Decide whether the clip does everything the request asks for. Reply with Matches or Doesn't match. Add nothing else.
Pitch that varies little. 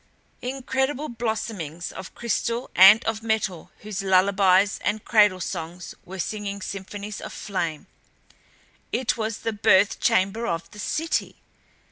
Doesn't match